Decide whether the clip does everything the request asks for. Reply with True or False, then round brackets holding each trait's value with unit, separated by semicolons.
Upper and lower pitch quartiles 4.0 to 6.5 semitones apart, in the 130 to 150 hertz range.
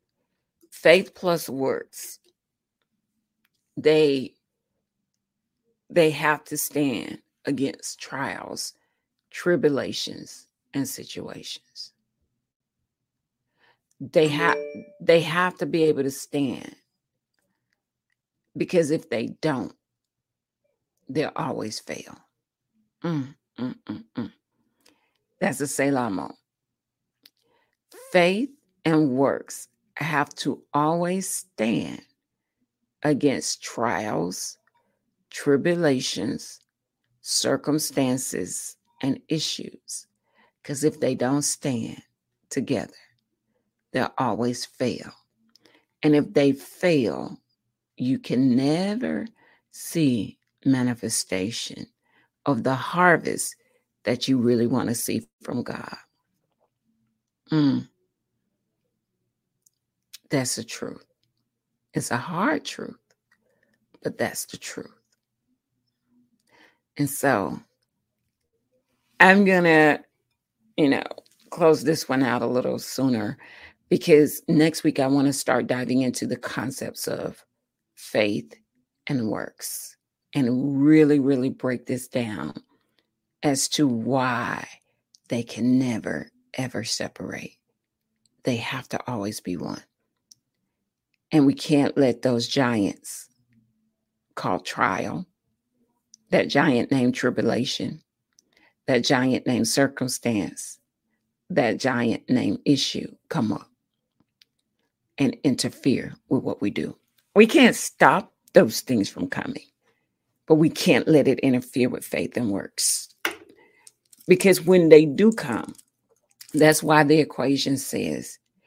True (4.7 semitones; 140 Hz)